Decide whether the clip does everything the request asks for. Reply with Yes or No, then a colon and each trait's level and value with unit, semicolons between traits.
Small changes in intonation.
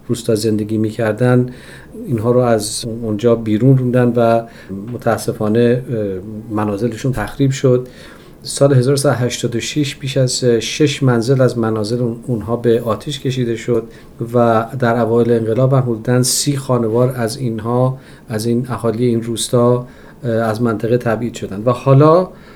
Yes: narrow, 1.8 semitones